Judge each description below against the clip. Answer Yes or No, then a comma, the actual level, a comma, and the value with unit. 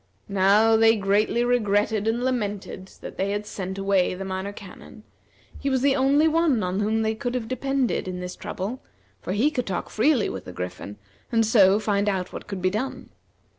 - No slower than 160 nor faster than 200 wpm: Yes, average, 195 wpm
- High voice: Yes, high, 210 Hz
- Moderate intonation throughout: Yes, average, 4.0 semitones